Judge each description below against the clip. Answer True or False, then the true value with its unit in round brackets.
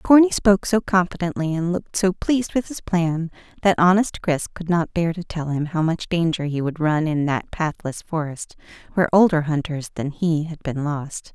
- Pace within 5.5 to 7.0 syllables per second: False (5.0 syllables/s)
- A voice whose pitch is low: False (170 Hz)